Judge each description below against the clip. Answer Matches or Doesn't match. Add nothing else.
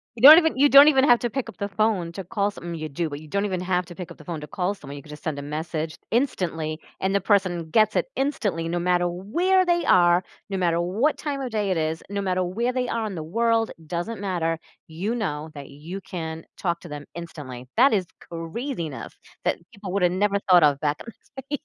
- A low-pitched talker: Doesn't match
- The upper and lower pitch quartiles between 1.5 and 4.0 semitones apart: Doesn't match